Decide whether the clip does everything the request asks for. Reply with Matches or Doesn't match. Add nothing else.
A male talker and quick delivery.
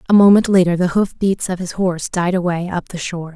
Doesn't match